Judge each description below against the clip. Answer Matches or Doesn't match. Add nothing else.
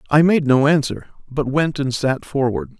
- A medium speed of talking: Matches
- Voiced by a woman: Doesn't match